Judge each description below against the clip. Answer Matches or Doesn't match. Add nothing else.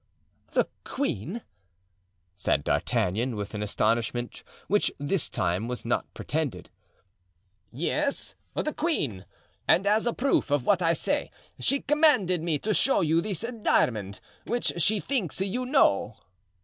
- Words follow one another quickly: Doesn't match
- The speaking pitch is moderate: Matches